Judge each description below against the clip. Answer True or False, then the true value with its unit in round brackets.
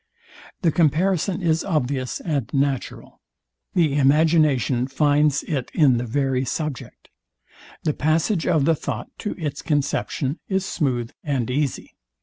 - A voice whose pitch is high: False (145 Hz)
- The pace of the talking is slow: True (130 wpm)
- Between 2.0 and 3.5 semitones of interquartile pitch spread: True (3.2 semitones)